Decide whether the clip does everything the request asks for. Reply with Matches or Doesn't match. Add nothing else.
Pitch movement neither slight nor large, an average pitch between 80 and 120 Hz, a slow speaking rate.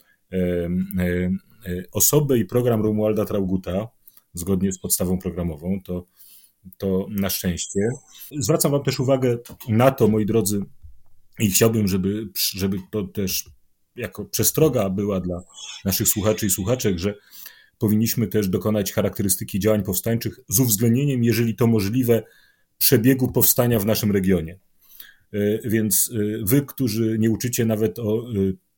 Doesn't match